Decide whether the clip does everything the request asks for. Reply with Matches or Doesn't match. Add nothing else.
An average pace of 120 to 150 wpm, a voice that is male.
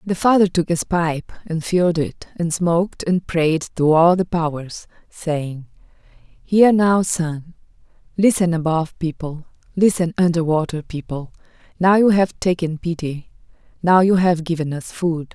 Doesn't match